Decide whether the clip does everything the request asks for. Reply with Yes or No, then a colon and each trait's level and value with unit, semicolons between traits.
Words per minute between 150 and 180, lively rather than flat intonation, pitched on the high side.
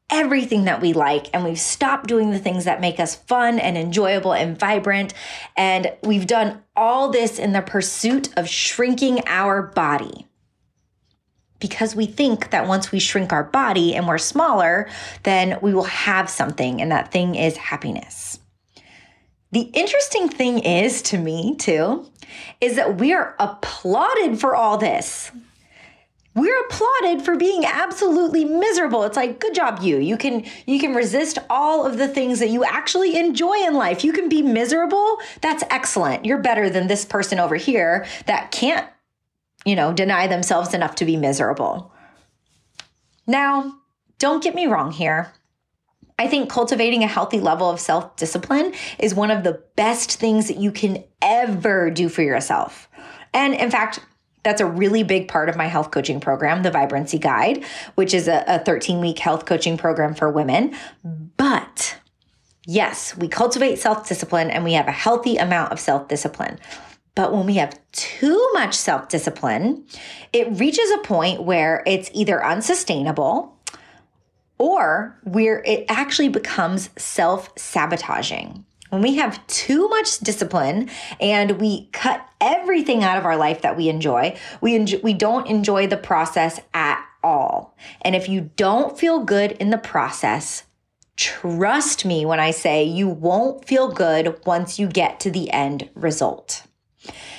Yes: average, 160 wpm; wide, 7.2 semitones; high, 210 Hz